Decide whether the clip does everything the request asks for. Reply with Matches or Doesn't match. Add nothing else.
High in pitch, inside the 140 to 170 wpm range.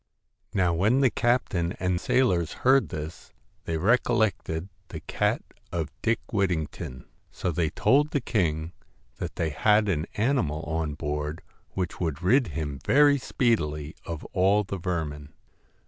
Doesn't match